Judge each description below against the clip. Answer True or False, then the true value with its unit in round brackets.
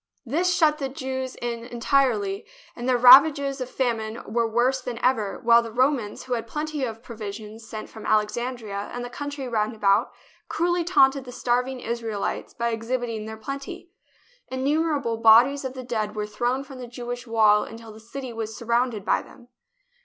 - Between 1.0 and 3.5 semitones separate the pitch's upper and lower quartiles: True (2.9 semitones)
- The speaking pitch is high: True (240 Hz)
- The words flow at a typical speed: True (190 wpm)